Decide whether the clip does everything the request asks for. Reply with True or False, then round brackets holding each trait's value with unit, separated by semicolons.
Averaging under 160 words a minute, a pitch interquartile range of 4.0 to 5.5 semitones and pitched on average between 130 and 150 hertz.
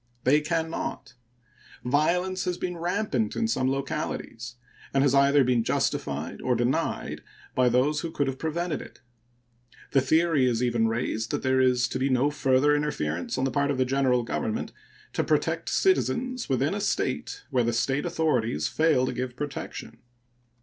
False (170 wpm; 4.3 semitones; 140 Hz)